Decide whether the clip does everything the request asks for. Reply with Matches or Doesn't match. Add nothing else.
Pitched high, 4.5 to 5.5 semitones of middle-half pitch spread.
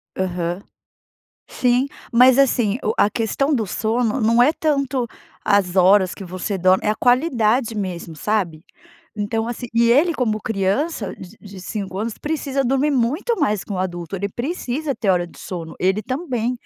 Matches